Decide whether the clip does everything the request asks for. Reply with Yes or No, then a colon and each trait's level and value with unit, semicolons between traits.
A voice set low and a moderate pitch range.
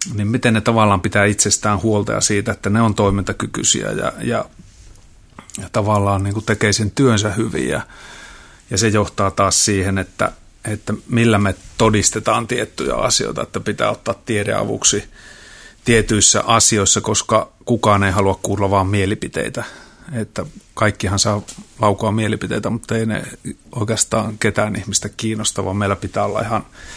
No: low, 105 Hz; narrow, 1.8 semitones